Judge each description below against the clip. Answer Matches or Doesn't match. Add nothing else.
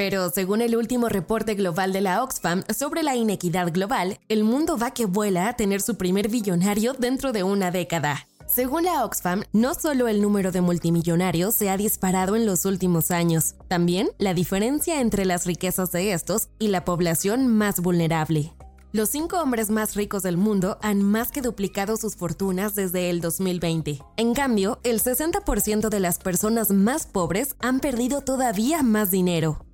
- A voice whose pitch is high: Matches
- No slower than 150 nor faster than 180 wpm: Matches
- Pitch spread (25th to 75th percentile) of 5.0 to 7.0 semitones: Doesn't match